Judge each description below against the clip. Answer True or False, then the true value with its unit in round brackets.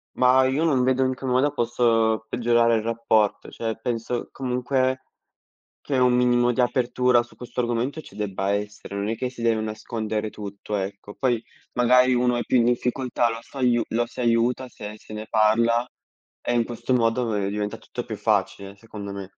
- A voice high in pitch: False (120 Hz)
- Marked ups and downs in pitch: False (2.5 semitones)